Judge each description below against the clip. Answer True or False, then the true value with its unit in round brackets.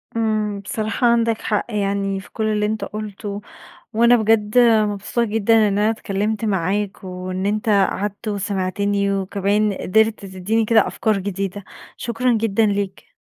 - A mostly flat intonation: True (1.9 semitones)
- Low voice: False (210 Hz)